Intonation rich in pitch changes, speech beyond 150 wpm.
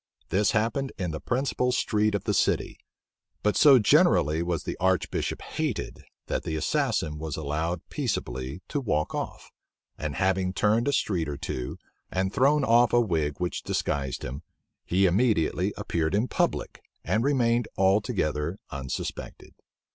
No: wide, 6.9 semitones; average, 145 wpm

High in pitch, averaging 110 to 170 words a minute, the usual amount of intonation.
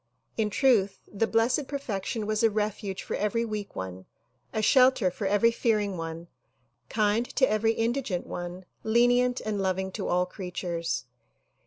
Yes: high, 210 Hz; average, 150 wpm; average, 3.6 semitones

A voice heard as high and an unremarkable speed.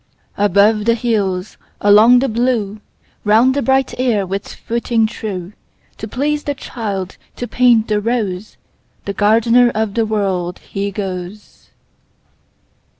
No: high, 215 Hz; slow, 115 wpm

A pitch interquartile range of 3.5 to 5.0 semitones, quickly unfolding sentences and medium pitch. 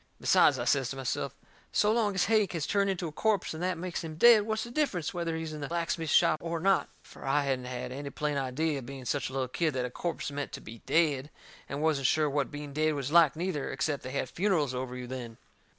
Yes: average, 4.2 semitones; fast, 245 wpm; medium, 150 Hz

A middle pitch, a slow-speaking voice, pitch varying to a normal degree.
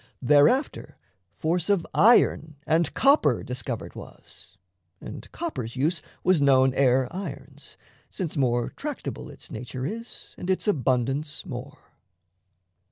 No: medium, 150 Hz; slow, 115 wpm; wide, 6.1 semitones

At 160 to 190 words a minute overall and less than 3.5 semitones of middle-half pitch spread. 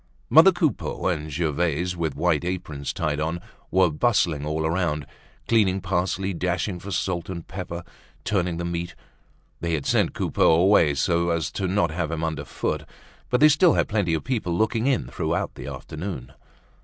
Yes: average, 165 wpm; average, 2.9 semitones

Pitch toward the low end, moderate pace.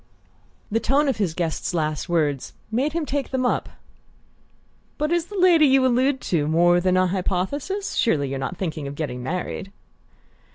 No: high, 190 Hz; average, 170 wpm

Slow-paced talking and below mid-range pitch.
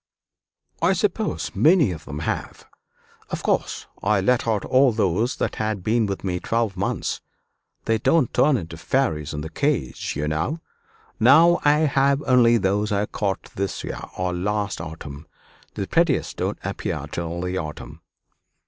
No: average, 155 wpm; low, 105 Hz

